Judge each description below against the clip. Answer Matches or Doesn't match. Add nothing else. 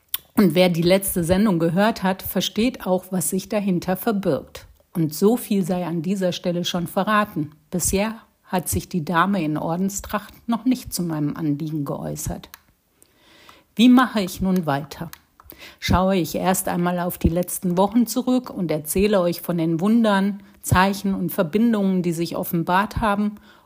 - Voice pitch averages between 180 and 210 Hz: Matches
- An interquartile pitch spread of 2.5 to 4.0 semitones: Matches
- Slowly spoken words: Doesn't match